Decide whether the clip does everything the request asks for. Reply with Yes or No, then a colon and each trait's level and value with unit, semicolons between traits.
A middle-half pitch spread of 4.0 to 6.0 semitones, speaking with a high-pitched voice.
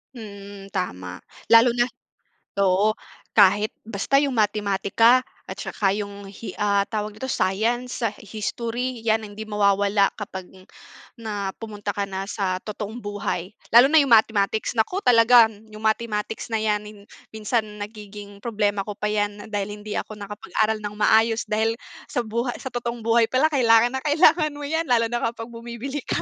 No: narrow, 2.4 semitones; high, 215 Hz